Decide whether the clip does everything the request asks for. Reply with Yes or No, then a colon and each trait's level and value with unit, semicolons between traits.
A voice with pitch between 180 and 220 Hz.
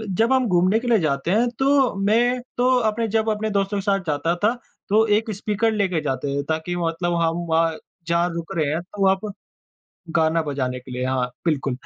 Yes: medium, 185 Hz